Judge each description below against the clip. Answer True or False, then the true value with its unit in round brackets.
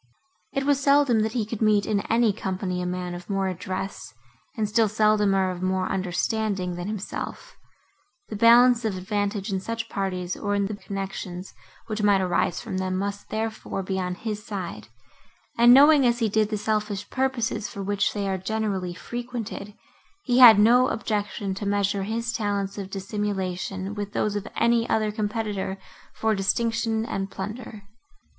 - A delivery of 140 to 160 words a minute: False (170 wpm)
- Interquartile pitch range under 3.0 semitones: True (2.6 semitones)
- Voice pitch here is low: False (205 Hz)